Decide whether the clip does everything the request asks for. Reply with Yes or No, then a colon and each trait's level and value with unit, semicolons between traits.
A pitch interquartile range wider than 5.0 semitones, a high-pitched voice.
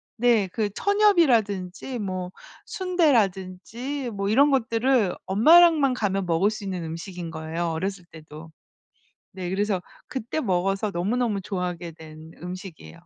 Yes: wide, 5.5 semitones; high, 195 Hz